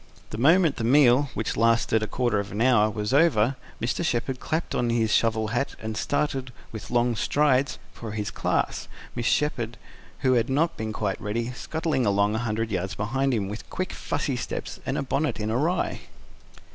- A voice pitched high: No, low, 120 Hz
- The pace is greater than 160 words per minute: Yes, average, 185 wpm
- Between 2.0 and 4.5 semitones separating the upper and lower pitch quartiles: Yes, average, 3.9 semitones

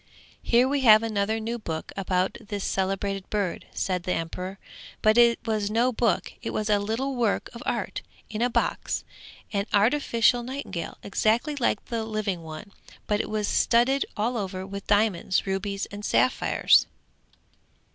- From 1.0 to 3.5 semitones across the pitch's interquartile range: Yes, average, 3.0 semitones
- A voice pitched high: Yes, high, 215 Hz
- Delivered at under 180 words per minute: Yes, average, 155 wpm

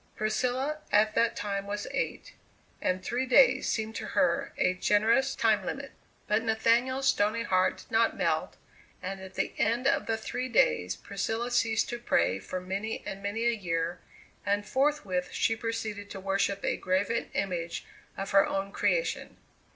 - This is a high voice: Yes, high, 215 Hz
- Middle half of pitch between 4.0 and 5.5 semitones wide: No, average, 3.5 semitones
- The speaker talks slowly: No, average, 165 wpm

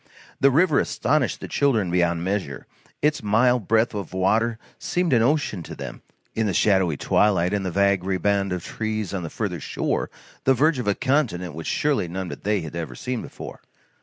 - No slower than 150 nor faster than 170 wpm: No, average, 195 wpm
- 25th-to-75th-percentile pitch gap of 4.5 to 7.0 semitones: Yes, average, 5.2 semitones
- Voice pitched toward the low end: Yes, low, 100 Hz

